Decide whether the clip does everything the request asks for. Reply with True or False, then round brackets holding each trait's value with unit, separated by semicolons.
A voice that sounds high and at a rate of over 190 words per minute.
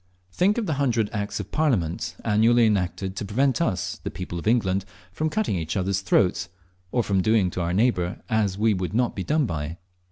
False (100 Hz; 200 wpm)